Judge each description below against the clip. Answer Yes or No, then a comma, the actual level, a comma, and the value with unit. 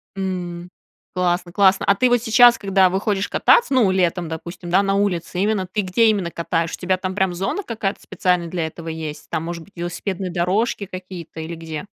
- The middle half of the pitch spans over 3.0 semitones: No, narrow, 2.6 semitones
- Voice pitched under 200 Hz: Yes, medium, 185 Hz